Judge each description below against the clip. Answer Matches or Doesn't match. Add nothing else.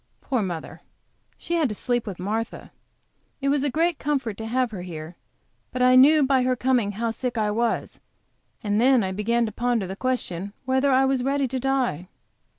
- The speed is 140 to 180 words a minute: Doesn't match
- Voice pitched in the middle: Doesn't match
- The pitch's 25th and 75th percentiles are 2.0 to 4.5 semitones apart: Matches